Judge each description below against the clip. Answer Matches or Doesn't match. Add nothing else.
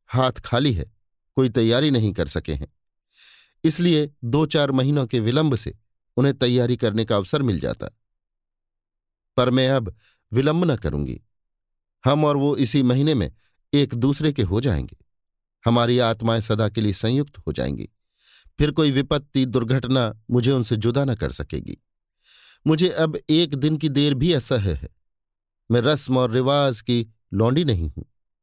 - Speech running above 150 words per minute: Matches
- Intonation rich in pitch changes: Matches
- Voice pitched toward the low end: Matches